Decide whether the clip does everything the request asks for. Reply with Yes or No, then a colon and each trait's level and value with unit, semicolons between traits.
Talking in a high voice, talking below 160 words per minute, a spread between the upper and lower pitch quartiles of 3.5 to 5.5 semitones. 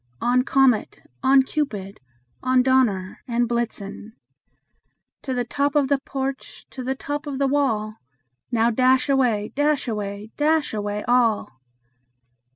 Yes: very high, 255 Hz; slow, 135 wpm; average, 3.9 semitones